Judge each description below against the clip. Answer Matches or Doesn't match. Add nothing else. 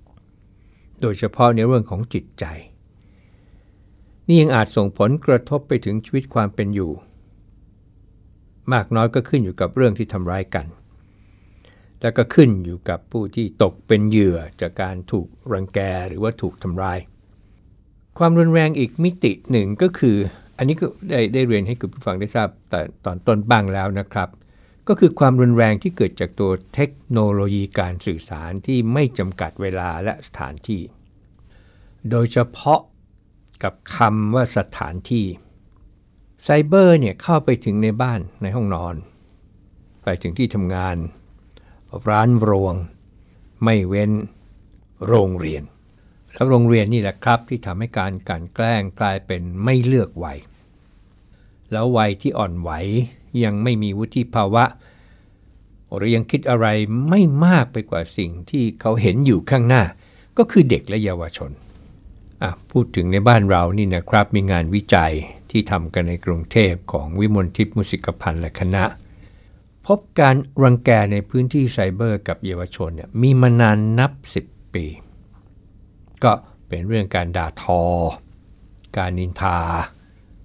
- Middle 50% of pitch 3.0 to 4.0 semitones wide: Matches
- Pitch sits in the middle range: Doesn't match